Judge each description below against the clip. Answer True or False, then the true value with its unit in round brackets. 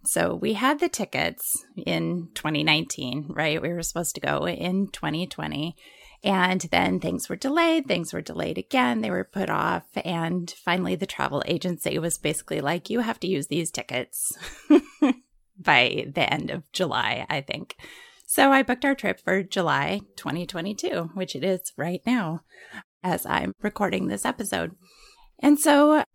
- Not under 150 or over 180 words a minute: True (160 wpm)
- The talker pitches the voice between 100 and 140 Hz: False (185 Hz)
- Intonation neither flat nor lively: False (7.4 semitones)